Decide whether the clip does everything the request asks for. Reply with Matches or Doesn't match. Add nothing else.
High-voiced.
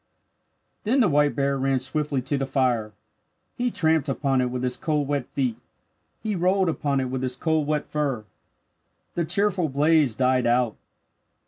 Doesn't match